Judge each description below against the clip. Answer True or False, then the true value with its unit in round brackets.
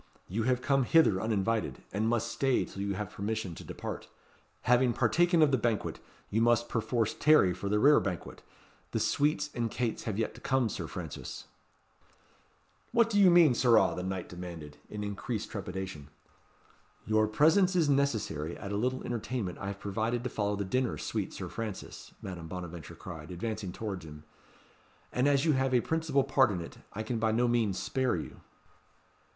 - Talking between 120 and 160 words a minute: False (175 wpm)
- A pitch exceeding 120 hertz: False (110 Hz)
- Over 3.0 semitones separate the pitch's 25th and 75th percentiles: True (4.9 semitones)